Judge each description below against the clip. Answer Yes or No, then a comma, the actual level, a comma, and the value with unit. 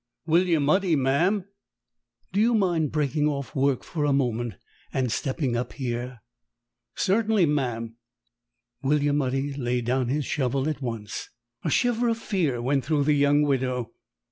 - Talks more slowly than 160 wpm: Yes, average, 145 wpm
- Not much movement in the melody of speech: No, average, 3.9 semitones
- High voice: No, medium, 140 Hz